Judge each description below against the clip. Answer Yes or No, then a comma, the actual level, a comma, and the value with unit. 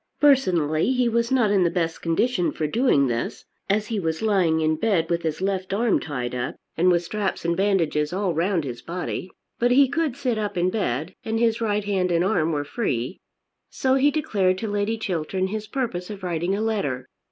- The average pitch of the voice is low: No, high, 190 Hz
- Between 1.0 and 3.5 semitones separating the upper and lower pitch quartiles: No, average, 5.2 semitones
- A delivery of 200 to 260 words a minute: Yes, fast, 205 wpm